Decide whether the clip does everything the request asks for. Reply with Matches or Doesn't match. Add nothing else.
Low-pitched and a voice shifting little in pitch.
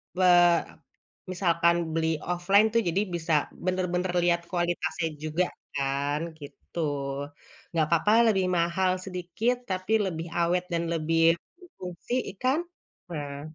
Doesn't match